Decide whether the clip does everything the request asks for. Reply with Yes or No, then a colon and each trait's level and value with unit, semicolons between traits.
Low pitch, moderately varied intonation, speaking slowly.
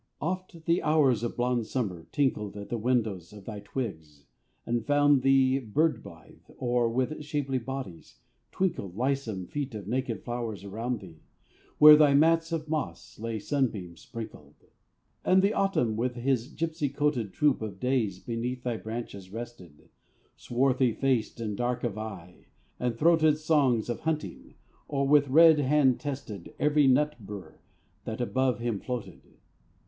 No: low, 125 Hz; average, 4.8 semitones; average, 150 wpm